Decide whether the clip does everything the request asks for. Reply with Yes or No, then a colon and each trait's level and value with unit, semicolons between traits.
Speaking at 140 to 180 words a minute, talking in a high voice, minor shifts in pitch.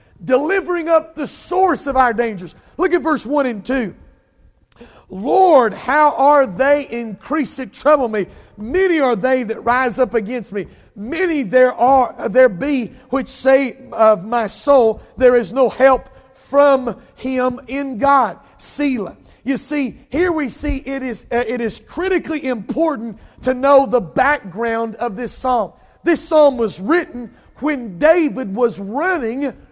No: average, 150 wpm; very high, 260 Hz; average, 3.5 semitones